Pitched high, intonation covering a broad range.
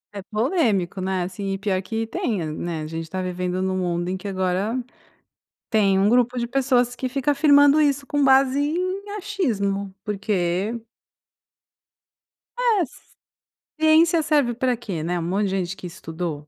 Yes: high, 210 Hz; wide, 6.7 semitones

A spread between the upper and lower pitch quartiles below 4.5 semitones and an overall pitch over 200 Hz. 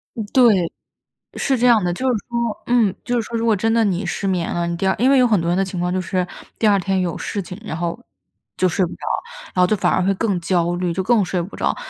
No: average, 4.1 semitones; high, 190 Hz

